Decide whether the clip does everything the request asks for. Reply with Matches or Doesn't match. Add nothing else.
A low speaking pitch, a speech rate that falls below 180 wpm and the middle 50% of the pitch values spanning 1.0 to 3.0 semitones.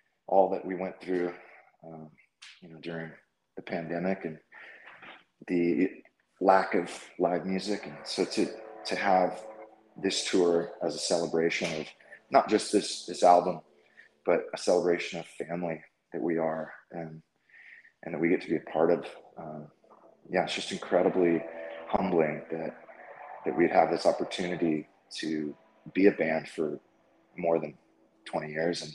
Matches